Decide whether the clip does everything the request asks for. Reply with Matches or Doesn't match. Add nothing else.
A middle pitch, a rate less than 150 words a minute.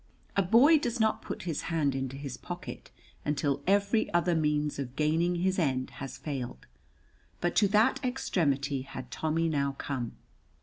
Doesn't match